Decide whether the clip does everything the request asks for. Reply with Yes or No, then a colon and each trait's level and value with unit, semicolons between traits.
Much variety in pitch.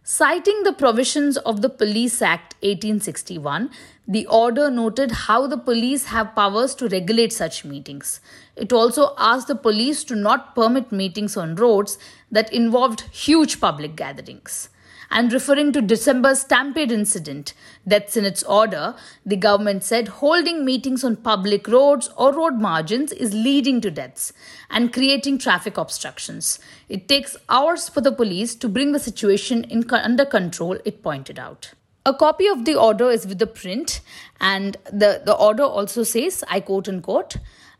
No: average, 4.8 semitones